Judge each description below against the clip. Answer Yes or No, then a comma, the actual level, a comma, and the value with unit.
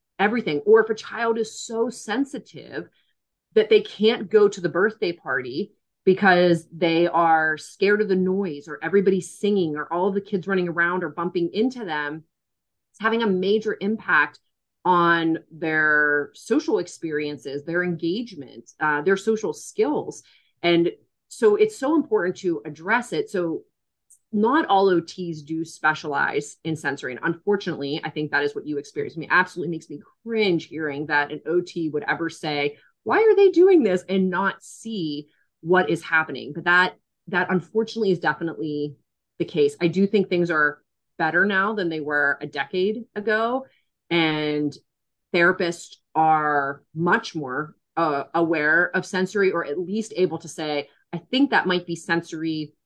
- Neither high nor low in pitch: Yes, medium, 170 Hz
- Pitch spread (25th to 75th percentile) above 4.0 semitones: Yes, average, 4.7 semitones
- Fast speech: No, average, 165 wpm